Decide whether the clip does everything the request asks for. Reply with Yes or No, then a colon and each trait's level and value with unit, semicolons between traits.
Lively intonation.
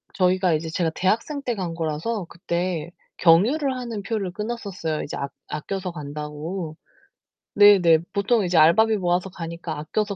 No: average, 4.0 semitones